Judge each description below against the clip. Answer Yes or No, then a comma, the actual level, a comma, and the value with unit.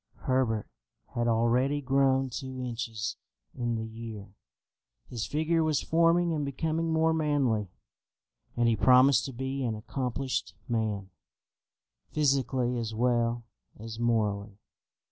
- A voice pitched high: No, low, 125 Hz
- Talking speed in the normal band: No, slow, 120 wpm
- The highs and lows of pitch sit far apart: No, average, 3.5 semitones